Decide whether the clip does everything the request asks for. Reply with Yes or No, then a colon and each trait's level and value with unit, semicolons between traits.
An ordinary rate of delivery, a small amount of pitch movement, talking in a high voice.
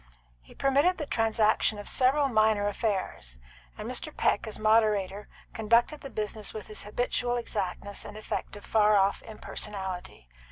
Yes: average, 150 wpm; narrow, 2.3 semitones; high, 215 Hz